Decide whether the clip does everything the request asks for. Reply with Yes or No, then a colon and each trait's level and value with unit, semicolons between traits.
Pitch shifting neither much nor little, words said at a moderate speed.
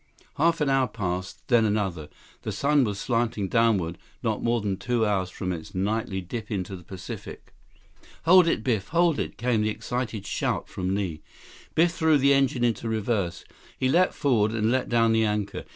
Yes: average, 4.7 semitones; average, 185 wpm